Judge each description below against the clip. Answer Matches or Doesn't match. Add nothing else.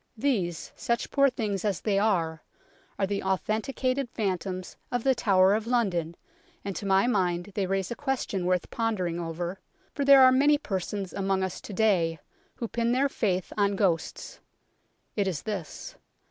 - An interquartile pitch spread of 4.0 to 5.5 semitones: Matches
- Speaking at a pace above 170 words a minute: Doesn't match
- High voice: Matches